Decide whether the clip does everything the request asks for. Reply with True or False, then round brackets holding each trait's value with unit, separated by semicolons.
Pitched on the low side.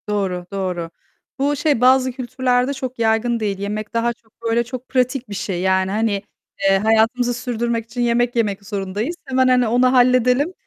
False (235 Hz)